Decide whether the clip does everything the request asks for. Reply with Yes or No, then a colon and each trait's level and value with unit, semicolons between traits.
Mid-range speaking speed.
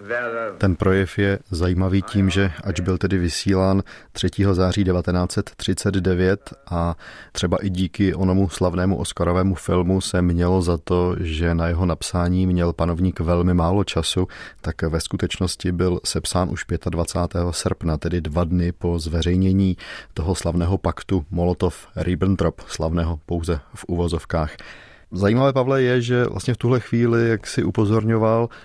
Yes: average, 140 wpm